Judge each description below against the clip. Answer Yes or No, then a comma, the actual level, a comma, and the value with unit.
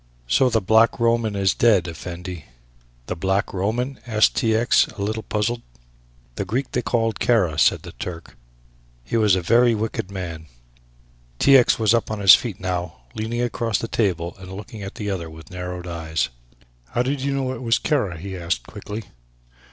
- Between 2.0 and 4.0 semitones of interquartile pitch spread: No, average, 4.5 semitones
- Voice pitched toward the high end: No, low, 105 Hz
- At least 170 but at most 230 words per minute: Yes, average, 185 wpm